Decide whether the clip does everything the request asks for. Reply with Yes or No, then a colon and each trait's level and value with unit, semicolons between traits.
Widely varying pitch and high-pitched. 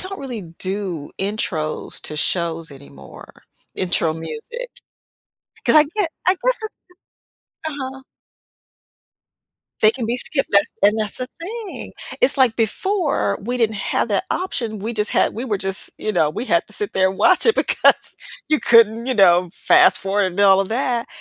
Yes: wide, 6.1 semitones; high, 220 Hz